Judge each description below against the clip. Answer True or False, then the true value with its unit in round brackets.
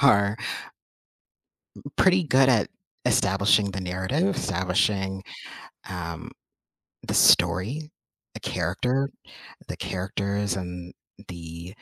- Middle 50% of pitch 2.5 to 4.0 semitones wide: False (5.4 semitones)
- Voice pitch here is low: True (100 Hz)